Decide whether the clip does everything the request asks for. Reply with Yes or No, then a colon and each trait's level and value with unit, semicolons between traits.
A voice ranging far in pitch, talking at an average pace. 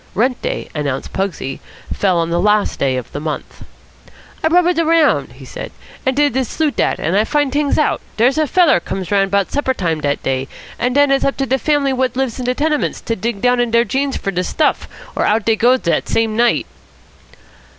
No: wide, 6.3 semitones; fast, 220 wpm